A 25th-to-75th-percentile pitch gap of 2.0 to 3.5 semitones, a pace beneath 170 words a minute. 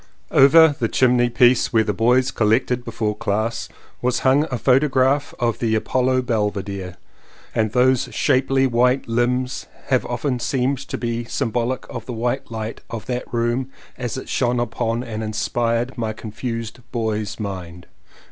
Yes: narrow, 2.4 semitones; average, 155 wpm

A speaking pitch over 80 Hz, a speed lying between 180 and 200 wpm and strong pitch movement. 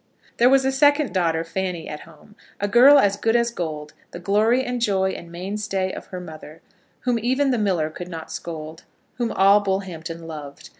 Yes: high, 190 Hz; average, 190 wpm; wide, 6.1 semitones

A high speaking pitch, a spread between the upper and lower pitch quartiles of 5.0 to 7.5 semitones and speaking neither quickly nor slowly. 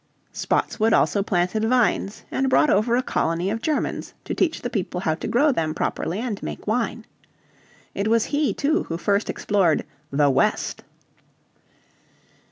Yes: high, 215 Hz; wide, 5.4 semitones; average, 155 wpm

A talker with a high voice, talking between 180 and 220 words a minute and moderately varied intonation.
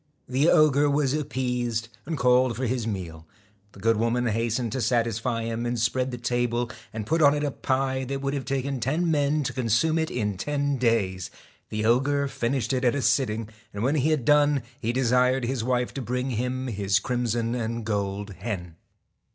No: low, 125 Hz; average, 190 wpm; average, 3.1 semitones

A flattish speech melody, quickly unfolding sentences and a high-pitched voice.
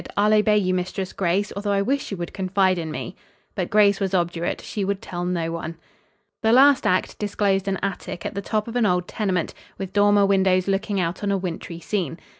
Yes: narrow, 2.3 semitones; fast, 215 wpm; high, 195 Hz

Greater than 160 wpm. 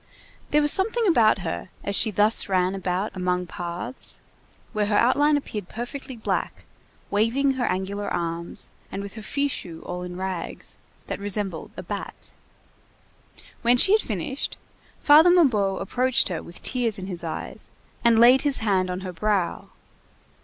No: average, 155 wpm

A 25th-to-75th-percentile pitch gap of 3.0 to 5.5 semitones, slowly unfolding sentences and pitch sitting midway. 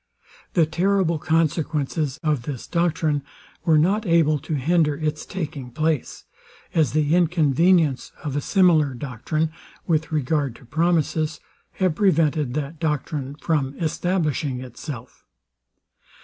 No: narrow, 2.6 semitones; slow, 120 wpm; medium, 155 Hz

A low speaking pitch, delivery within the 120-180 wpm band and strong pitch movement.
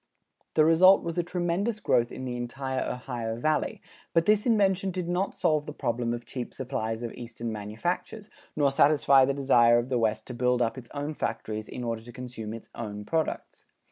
No: low, 130 Hz; average, 195 wpm; wide, 5.7 semitones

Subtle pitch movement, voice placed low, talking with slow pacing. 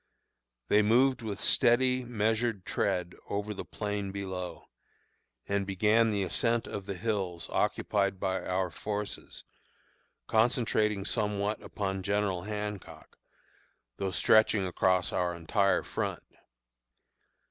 Yes: narrow, 2.3 semitones; low, 100 Hz; slow, 110 wpm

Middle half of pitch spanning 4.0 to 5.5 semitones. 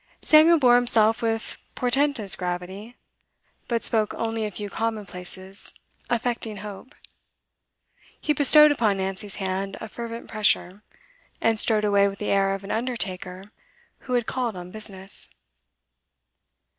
No: average, 3.4 semitones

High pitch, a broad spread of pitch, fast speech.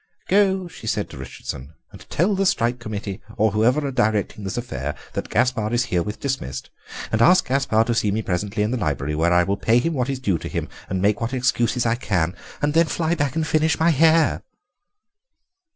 No: low, 115 Hz; wide, 6.0 semitones; fast, 210 wpm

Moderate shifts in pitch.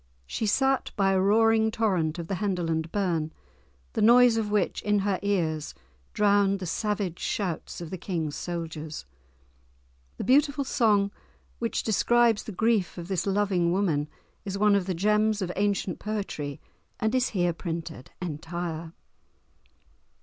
Yes: average, 3.9 semitones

